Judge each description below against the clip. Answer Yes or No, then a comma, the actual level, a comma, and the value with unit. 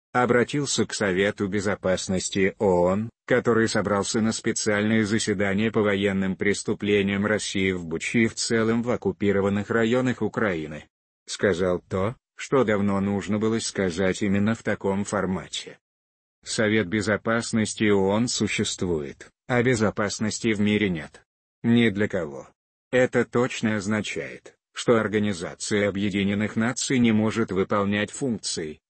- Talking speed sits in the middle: Yes, average, 120 wpm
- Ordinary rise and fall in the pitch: No, narrow, 2.2 semitones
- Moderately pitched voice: No, low, 105 Hz